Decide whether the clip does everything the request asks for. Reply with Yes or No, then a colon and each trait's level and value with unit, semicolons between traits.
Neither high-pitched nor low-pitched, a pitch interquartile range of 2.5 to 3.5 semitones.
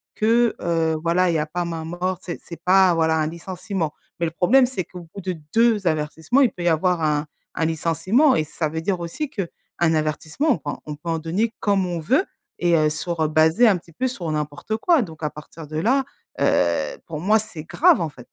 No: medium, 170 Hz; average, 4.0 semitones